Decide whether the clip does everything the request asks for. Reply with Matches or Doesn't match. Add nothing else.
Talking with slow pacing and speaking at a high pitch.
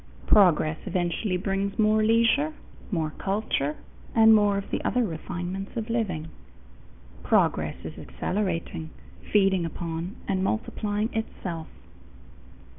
Matches